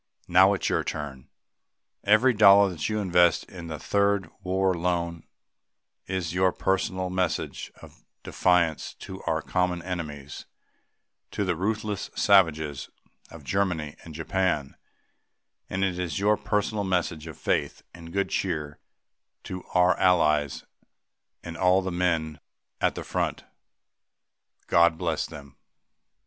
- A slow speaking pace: Yes, slow, 130 wpm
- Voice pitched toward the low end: Yes, very low, 90 Hz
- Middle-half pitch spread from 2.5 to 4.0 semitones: Yes, average, 2.9 semitones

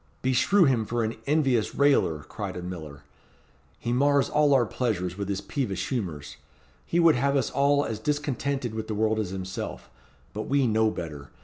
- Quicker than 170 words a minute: Yes, average, 180 wpm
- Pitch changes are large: Yes, wide, 6.4 semitones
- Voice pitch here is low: Yes, low, 115 Hz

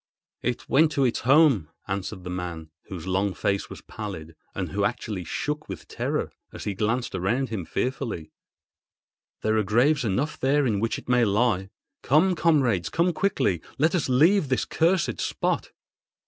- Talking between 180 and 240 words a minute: No, average, 160 wpm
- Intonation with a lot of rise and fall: Yes, wide, 7.1 semitones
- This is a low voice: Yes, low, 115 Hz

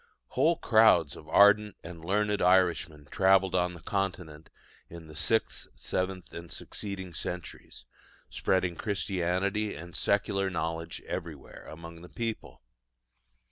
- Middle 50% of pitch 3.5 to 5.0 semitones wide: No, average, 2.9 semitones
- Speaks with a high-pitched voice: No, very low, 90 Hz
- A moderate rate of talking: No, slow, 120 wpm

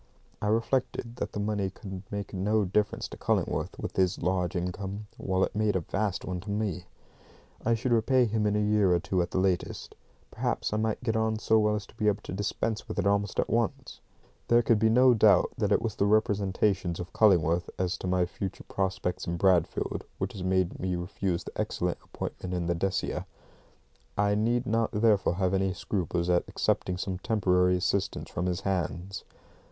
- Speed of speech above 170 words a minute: Yes, average, 200 wpm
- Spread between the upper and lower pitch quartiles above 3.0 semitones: No, average, 2.7 semitones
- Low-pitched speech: Yes, low, 100 Hz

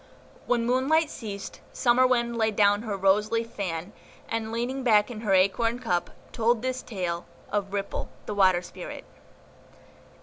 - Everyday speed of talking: Yes, average, 155 wpm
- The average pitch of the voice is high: Yes, high, 220 Hz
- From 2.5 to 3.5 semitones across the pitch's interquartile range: Yes, average, 3.2 semitones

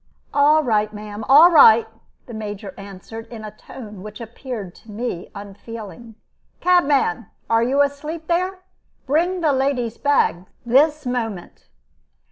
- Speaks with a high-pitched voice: Yes, high, 235 Hz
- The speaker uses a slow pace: Yes, slow, 130 wpm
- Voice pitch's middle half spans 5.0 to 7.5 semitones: Yes, average, 5.3 semitones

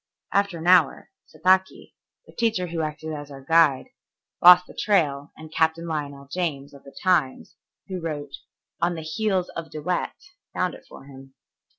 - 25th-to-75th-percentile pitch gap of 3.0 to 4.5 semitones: Yes, average, 3.8 semitones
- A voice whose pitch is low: No, medium, 160 Hz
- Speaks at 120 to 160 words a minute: No, average, 170 wpm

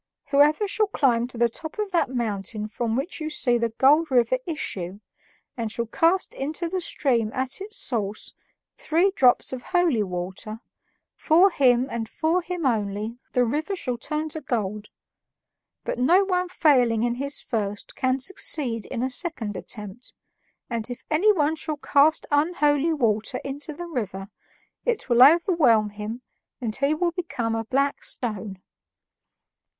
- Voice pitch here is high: Yes, very high, 260 Hz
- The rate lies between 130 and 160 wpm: Yes, average, 155 wpm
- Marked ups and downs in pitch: Yes, wide, 5.8 semitones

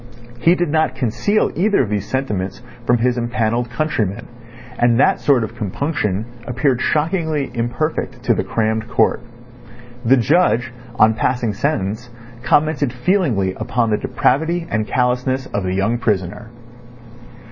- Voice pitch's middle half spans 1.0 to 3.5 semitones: No, average, 4.7 semitones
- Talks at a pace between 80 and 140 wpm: Yes, slow, 135 wpm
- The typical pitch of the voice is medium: No, low, 120 Hz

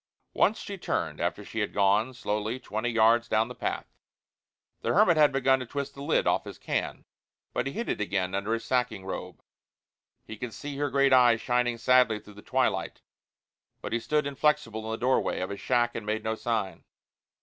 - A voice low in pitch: Yes, low, 120 Hz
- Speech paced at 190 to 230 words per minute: Yes, average, 200 wpm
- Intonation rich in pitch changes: No, average, 3.9 semitones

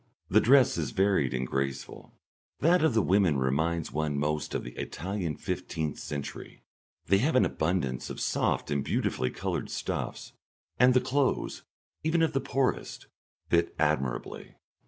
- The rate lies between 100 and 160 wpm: Yes, average, 150 wpm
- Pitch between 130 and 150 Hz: No, very low, 85 Hz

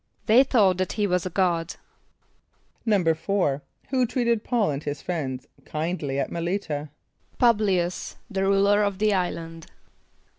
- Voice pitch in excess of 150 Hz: Yes, medium, 185 Hz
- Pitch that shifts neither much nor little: Yes, average, 4.1 semitones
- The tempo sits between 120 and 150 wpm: Yes, average, 145 wpm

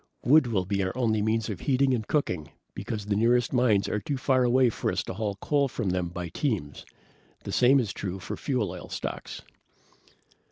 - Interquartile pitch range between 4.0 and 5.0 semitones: Yes, average, 4.6 semitones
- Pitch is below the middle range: Yes, low, 110 Hz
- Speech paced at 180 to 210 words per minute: Yes, average, 200 wpm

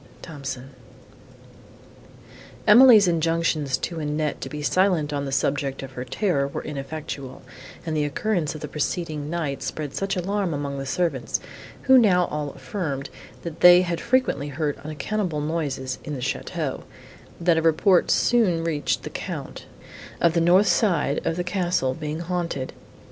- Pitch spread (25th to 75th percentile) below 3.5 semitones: No, average, 3.8 semitones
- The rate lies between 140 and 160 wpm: Yes, average, 155 wpm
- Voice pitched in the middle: Yes, medium, 155 Hz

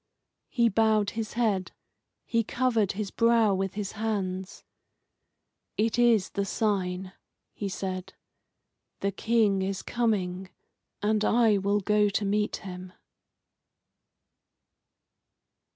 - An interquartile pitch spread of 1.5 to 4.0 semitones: Yes, narrow, 2.6 semitones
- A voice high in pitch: Yes, high, 205 Hz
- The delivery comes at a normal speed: No, slow, 105 wpm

